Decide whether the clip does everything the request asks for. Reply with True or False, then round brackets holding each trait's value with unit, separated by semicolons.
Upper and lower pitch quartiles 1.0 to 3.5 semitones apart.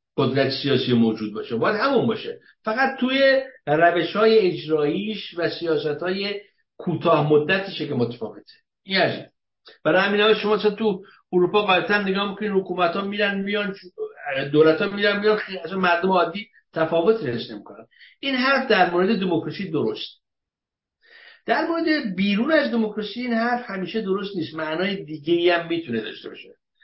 False (4.7 semitones)